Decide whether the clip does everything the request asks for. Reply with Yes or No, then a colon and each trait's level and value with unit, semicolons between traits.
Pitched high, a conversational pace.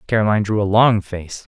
No: low, 105 Hz; average, 195 wpm